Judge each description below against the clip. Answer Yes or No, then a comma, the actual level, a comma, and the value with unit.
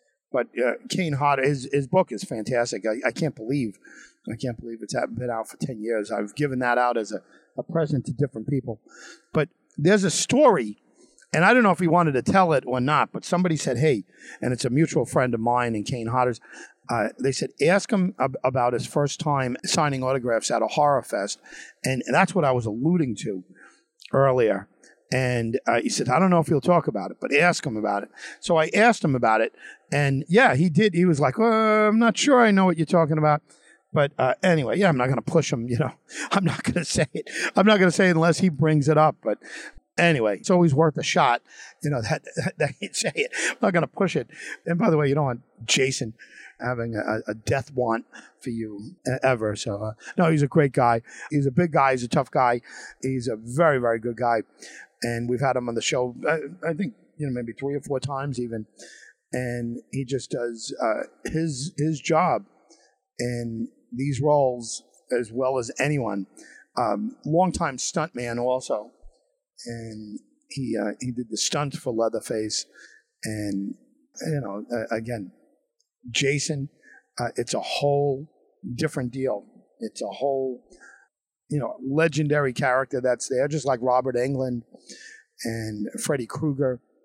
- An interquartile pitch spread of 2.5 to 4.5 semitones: No, average, 5.2 semitones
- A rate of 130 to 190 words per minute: No, average, 200 wpm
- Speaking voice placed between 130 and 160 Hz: Yes, low, 135 Hz